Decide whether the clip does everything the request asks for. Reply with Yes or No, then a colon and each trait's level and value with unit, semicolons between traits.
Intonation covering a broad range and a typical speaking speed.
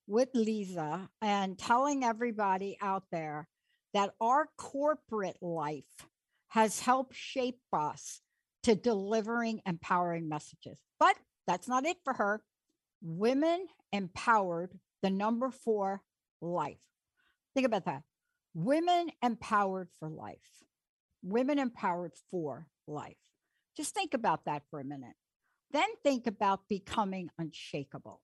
No: wide, 6.5 semitones; slow, 115 wpm